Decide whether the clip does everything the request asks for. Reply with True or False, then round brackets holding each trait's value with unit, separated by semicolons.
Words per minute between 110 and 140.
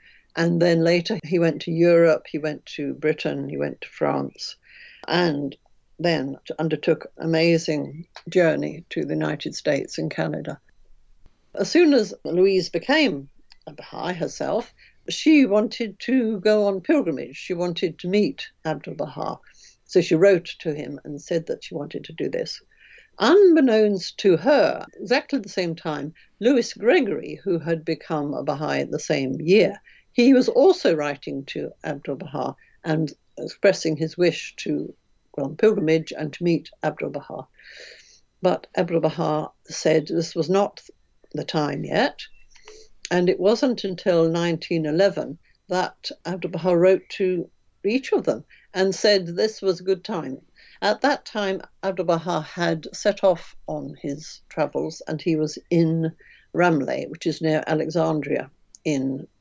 False (150 wpm)